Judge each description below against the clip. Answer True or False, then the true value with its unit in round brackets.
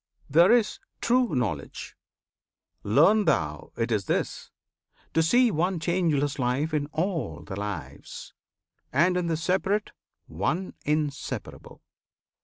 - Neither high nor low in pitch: True (155 Hz)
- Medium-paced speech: False (115 wpm)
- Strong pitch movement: True (6.4 semitones)